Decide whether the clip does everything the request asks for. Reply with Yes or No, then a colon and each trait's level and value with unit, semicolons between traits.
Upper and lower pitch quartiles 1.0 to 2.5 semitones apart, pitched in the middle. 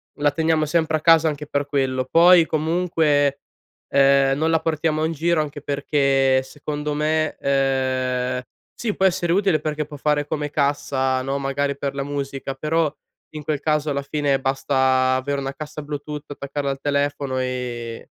Yes: narrow, 2.1 semitones; medium, 145 Hz